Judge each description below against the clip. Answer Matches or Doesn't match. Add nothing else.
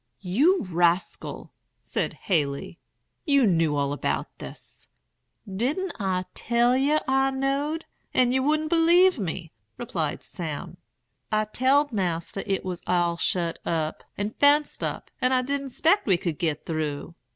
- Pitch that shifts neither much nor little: Doesn't match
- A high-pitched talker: Matches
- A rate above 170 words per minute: Doesn't match